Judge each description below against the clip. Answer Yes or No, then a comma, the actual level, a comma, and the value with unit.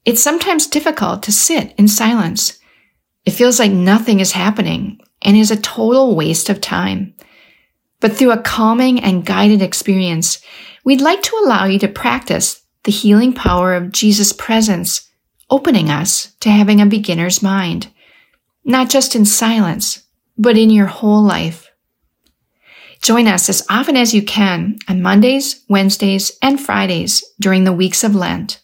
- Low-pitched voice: No, high, 210 Hz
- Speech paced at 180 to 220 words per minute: No, average, 155 wpm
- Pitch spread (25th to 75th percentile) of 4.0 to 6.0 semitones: No, average, 3.6 semitones